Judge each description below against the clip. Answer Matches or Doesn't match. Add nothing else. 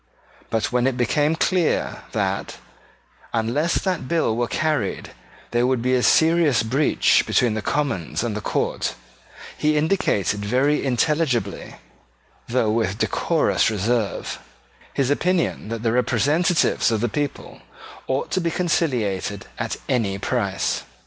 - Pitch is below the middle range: Matches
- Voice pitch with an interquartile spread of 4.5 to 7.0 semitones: Matches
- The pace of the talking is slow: Matches